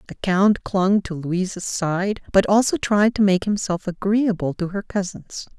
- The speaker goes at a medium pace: Yes, average, 170 wpm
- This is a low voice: No, high, 190 Hz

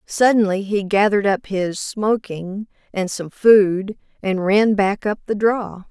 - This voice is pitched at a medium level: No, high, 200 Hz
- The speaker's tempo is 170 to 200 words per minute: No, average, 150 wpm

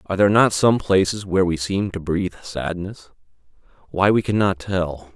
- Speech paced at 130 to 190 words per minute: Yes, average, 165 wpm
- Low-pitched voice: Yes, very low, 95 Hz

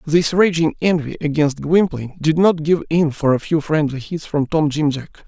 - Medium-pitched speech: Yes, medium, 155 Hz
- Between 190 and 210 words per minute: Yes, fast, 205 wpm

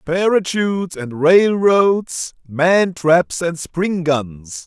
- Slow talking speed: Yes, slow, 105 wpm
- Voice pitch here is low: No, medium, 170 Hz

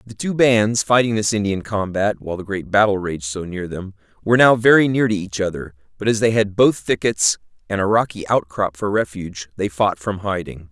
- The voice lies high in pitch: No, low, 100 Hz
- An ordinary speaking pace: No, fast, 215 wpm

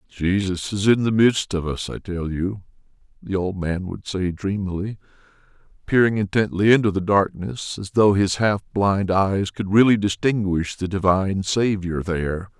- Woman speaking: No, male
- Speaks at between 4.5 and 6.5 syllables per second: Yes, 4.6 syllables/s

